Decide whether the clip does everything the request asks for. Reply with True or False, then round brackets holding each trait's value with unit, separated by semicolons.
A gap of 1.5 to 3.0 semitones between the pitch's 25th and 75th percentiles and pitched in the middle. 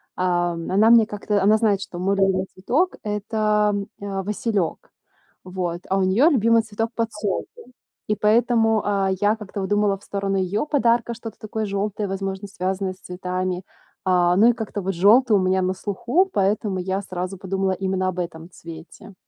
False (2.5 semitones; 200 Hz)